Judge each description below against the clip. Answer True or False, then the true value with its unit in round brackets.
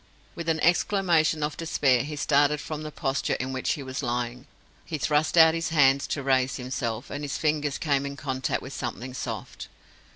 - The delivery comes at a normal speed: True (190 wpm)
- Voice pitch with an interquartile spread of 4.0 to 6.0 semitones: False (2.9 semitones)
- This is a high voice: False (140 Hz)